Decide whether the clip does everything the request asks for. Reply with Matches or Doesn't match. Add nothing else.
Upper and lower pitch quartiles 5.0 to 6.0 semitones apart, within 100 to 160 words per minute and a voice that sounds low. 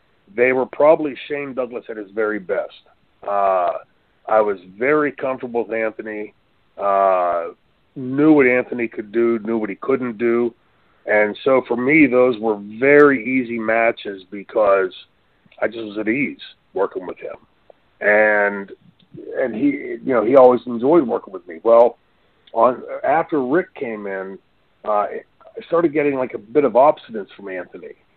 Matches